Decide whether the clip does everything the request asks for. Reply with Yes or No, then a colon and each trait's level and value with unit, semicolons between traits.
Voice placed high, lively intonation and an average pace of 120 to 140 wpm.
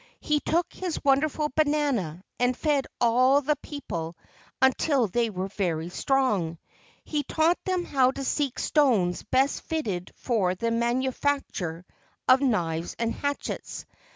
Yes: very high, 255 Hz; wide, 7.0 semitones; slow, 135 wpm